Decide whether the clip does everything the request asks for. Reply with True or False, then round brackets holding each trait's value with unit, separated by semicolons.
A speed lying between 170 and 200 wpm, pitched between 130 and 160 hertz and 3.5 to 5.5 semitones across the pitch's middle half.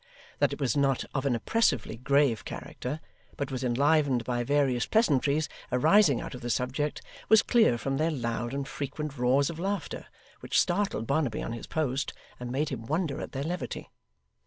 True (180 wpm; 140 Hz; 3.8 semitones)